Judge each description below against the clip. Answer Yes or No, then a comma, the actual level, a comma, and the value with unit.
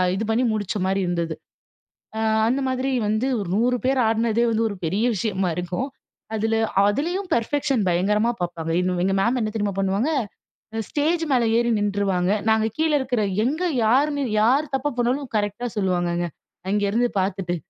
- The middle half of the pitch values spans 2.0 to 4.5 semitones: No, average, 4.9 semitones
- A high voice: Yes, high, 220 Hz